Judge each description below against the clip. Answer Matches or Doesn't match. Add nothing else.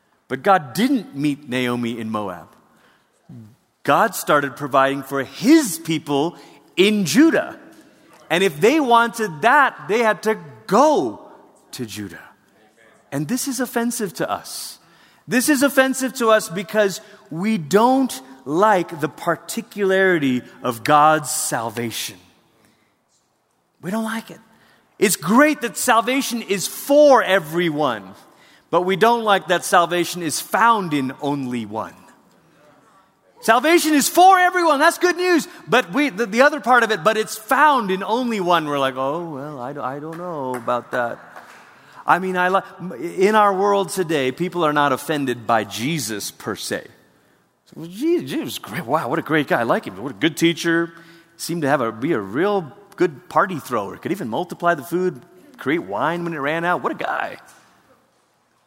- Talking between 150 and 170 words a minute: Matches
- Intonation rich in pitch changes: Matches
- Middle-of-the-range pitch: Matches